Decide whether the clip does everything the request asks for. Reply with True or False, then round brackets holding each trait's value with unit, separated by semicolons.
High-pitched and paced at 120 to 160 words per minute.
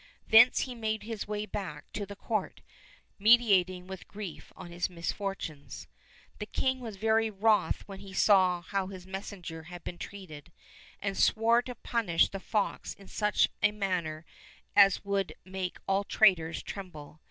True (195 Hz; 155 wpm)